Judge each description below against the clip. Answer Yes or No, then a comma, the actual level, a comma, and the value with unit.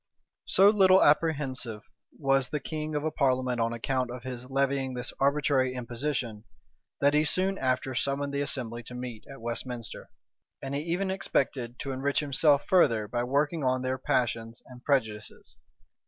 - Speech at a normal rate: Yes, average, 160 wpm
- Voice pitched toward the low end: Yes, low, 130 Hz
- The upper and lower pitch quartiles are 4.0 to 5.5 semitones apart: No, average, 2.9 semitones